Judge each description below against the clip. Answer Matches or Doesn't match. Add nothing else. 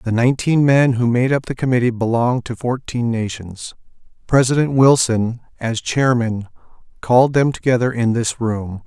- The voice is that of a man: Matches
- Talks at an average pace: Matches